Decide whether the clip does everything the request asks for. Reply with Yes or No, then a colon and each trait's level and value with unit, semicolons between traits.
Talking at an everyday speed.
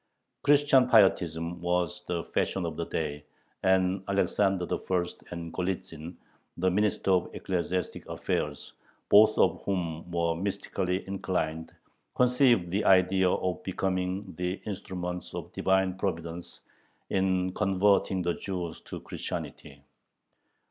No: slow, 115 wpm